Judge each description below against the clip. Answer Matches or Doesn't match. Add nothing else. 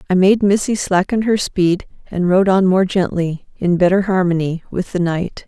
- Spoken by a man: Doesn't match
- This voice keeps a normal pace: Matches